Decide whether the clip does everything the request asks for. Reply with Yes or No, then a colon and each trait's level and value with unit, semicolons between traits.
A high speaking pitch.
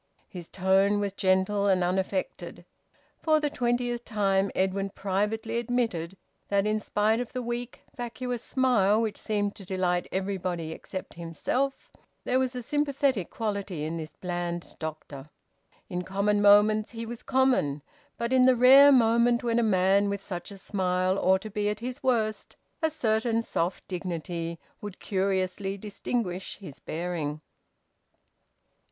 Yes: high, 205 Hz